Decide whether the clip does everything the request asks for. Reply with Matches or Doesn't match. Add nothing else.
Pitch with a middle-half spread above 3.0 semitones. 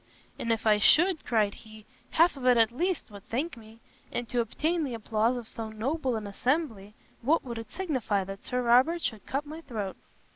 Matches